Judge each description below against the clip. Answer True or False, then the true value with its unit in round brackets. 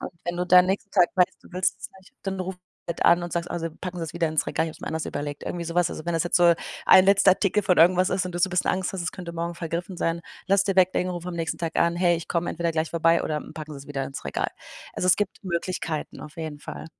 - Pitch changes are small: True (1.8 semitones)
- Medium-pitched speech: True (175 Hz)